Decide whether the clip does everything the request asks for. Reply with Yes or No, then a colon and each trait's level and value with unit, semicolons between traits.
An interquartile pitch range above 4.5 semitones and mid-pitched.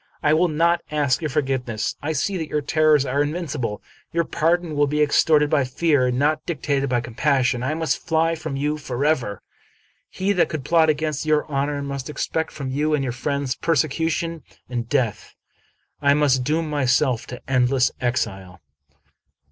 No: average, 3.2 semitones; medium, 145 Hz